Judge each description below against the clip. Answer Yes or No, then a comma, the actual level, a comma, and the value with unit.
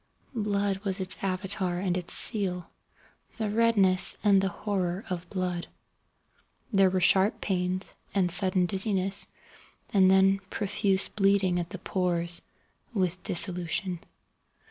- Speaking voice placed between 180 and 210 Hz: Yes, high, 190 Hz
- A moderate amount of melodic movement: No, narrow, 1.6 semitones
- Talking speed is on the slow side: Yes, slow, 120 wpm